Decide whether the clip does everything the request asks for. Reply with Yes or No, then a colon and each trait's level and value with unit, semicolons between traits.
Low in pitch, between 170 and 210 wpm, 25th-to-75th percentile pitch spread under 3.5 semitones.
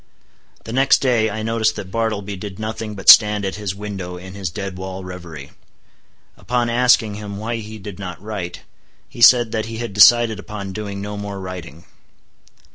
Yes: low, 105 Hz; average, 180 wpm; narrow, 2.6 semitones